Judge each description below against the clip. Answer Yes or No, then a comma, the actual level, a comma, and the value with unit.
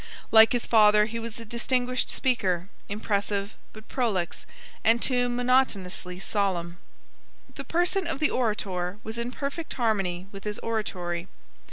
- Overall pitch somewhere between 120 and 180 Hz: No, high, 220 Hz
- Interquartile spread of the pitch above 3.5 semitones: Yes, average, 4.1 semitones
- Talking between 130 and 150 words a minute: Yes, average, 140 wpm